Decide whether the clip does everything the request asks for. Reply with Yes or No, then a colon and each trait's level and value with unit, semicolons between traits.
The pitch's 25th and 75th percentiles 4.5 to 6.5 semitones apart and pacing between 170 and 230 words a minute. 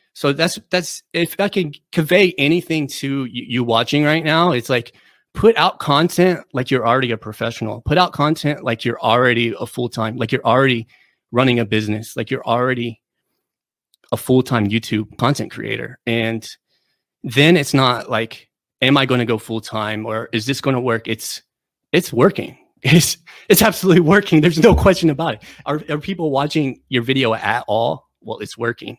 Yes: wide, 5.5 semitones; average, 180 wpm